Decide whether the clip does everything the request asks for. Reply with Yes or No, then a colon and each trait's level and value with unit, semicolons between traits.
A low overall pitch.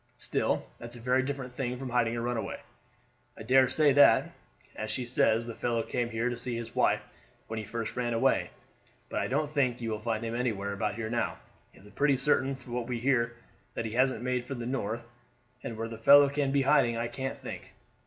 Yes: low, 120 Hz